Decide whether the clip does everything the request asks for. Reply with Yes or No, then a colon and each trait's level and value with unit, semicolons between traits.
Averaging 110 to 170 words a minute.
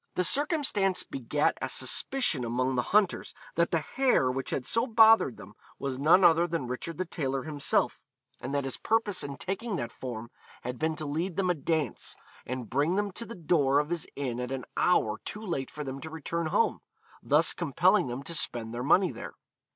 No: average, 200 wpm